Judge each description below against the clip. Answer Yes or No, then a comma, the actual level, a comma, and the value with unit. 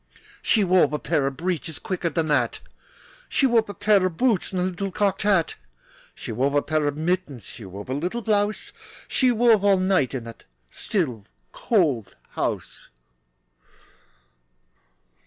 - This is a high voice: No, medium, 180 Hz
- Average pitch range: No, wide, 5.9 semitones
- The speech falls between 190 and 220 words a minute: No, average, 155 wpm